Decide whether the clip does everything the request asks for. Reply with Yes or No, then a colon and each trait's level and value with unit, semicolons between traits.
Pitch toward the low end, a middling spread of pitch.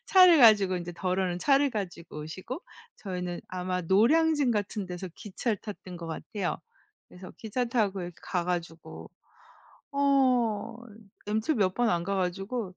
No: high, 195 Hz; average, 4.8 semitones